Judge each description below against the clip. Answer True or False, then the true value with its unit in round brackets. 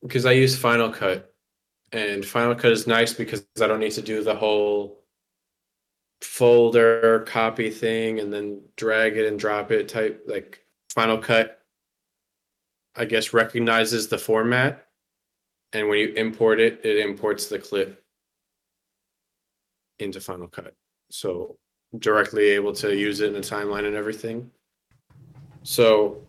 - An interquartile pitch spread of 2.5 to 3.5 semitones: True (2.9 semitones)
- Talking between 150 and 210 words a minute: False (140 wpm)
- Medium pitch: False (115 Hz)